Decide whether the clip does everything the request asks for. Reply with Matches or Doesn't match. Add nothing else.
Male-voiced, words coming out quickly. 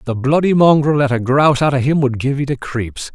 Matches